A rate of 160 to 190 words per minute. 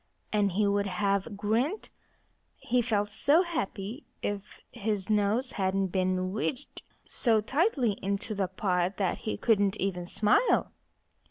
No: slow, 135 wpm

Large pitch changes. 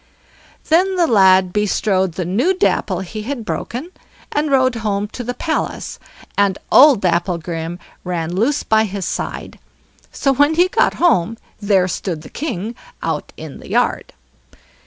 Yes: wide, 6.7 semitones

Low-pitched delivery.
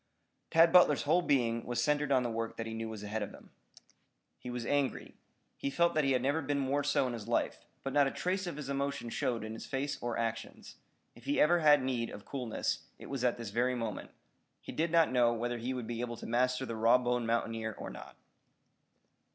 Yes: low, 125 Hz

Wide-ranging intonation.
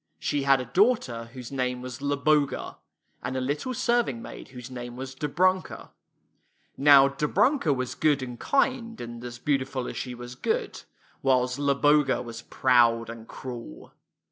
No: average, 3.1 semitones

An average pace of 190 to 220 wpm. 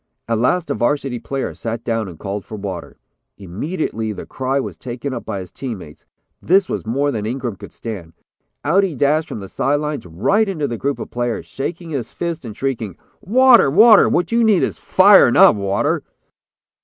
Yes: average, 195 wpm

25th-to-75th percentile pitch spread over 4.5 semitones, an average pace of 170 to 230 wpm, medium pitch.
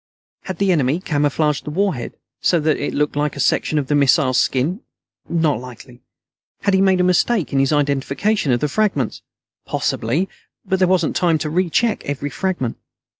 Yes: average, 4.9 semitones; average, 175 wpm; medium, 150 Hz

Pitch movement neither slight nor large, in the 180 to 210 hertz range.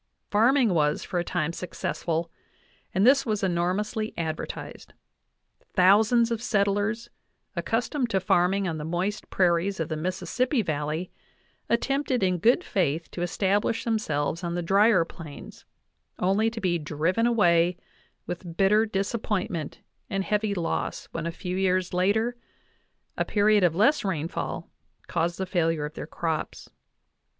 Yes: average, 4.2 semitones; medium, 185 Hz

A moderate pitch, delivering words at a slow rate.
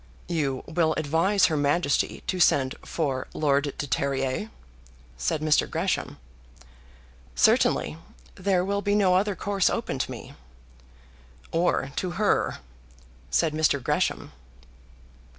Yes: medium, 155 Hz; slow, 115 wpm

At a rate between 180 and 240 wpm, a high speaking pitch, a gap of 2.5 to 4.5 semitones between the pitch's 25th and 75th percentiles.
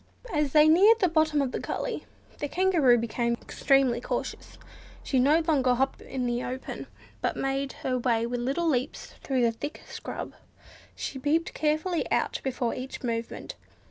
No: average, 165 wpm; very high, 270 Hz; average, 3.9 semitones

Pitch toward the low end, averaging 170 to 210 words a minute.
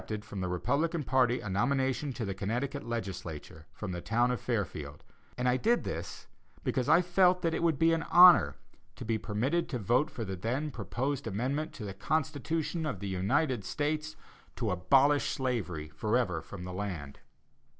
Yes: low, 125 Hz; average, 180 wpm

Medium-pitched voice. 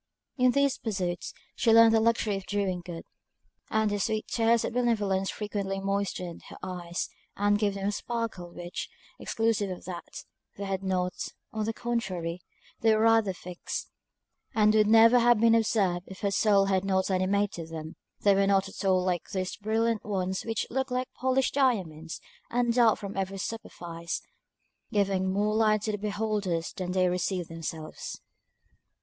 No: high, 200 Hz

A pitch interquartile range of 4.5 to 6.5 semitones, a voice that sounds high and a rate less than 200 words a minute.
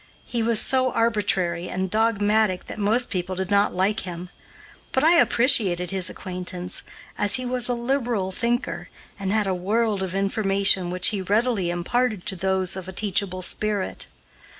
No: average, 3.6 semitones; high, 200 Hz; average, 165 wpm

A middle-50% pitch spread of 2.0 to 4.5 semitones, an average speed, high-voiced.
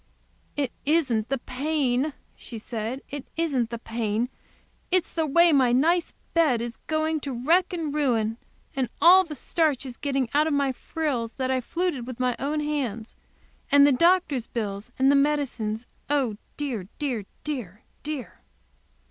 Yes: average, 4.2 semitones; average, 155 wpm; very high, 275 Hz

